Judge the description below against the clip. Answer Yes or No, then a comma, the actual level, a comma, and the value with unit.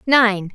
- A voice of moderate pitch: No, high, 220 Hz